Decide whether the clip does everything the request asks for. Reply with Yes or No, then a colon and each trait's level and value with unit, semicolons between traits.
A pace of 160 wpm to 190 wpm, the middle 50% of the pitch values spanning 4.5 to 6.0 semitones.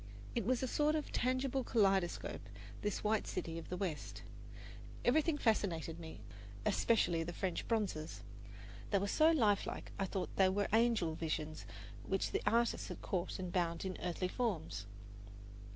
No: average, 150 wpm; wide, 5.4 semitones